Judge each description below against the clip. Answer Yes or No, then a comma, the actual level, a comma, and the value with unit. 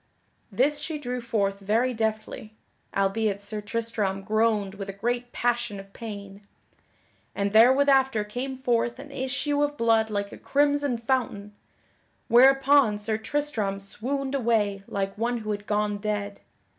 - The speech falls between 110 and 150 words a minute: Yes, average, 140 wpm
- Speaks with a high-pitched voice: Yes, high, 225 Hz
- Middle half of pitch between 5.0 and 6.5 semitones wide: No, average, 4.1 semitones